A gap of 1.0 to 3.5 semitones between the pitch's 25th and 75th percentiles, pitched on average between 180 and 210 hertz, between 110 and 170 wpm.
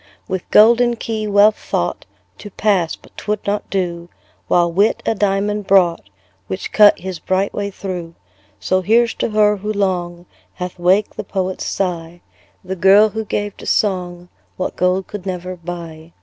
Yes: average, 2.8 semitones; high, 190 Hz; average, 165 wpm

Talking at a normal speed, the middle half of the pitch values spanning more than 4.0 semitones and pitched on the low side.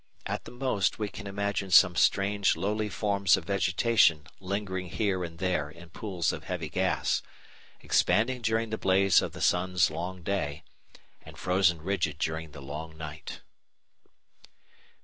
No: average, 150 wpm; average, 3.5 semitones; very low, 95 Hz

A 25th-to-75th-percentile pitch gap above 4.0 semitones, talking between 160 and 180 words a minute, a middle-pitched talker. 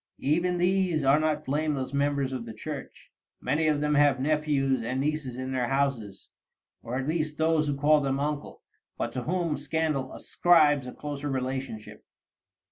No: narrow, 2.6 semitones; average, 165 wpm; medium, 145 Hz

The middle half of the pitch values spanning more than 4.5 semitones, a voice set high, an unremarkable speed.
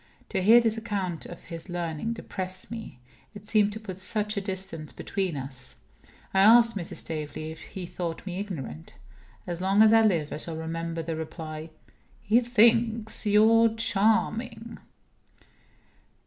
Yes: average, 5.0 semitones; high, 195 Hz; average, 150 wpm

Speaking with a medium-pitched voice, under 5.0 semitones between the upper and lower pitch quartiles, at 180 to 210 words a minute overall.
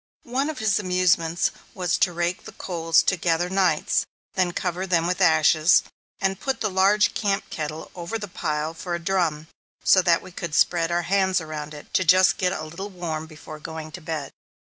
Yes: medium, 175 Hz; average, 2.8 semitones; average, 195 wpm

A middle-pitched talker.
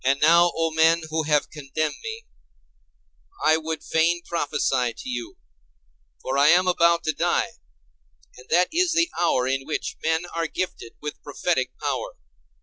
Yes: medium, 160 Hz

